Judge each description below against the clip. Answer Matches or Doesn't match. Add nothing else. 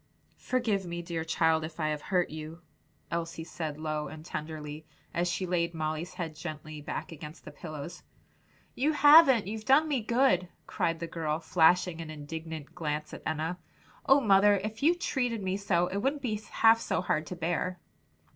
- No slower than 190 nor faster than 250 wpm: Doesn't match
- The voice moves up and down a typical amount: Matches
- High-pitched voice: Doesn't match